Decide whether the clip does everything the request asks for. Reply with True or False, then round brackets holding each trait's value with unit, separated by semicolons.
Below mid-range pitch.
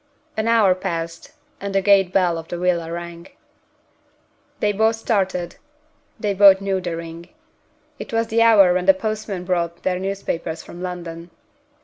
False (185 Hz)